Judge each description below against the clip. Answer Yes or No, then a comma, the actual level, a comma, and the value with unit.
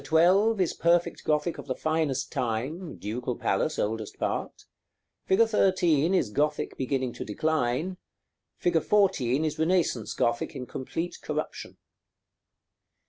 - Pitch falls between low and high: Yes, medium, 155 Hz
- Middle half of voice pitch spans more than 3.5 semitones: Yes, wide, 5.6 semitones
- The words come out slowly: Yes, slow, 125 wpm